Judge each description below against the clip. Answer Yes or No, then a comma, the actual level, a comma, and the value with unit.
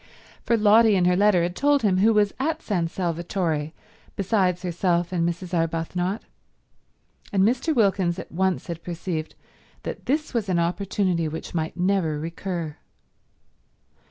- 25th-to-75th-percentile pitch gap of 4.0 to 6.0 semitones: No, average, 3.2 semitones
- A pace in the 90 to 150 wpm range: Yes, average, 145 wpm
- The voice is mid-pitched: Yes, medium, 180 Hz